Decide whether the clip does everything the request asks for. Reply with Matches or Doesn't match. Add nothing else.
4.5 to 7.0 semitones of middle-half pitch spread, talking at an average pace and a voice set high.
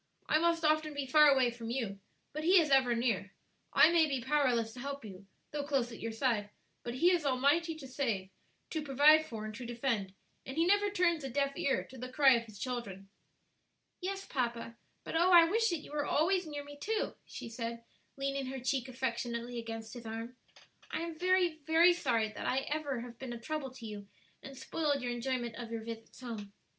Doesn't match